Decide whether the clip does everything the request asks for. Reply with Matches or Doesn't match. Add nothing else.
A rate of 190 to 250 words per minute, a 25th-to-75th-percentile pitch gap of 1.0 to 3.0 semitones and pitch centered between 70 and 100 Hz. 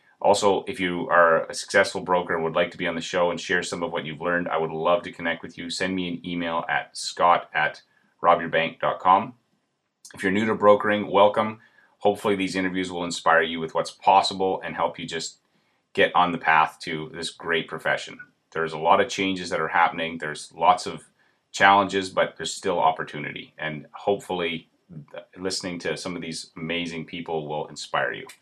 Matches